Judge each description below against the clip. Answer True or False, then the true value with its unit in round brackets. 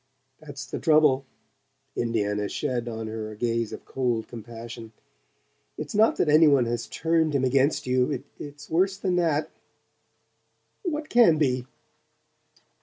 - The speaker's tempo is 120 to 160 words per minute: True (140 wpm)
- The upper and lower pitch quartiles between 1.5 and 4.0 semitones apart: False (5.1 semitones)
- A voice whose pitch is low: True (130 Hz)